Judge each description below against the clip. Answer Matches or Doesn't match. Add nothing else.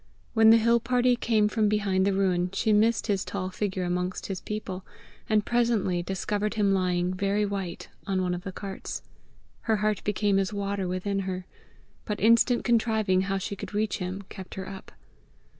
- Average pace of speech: Matches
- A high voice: Matches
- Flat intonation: Matches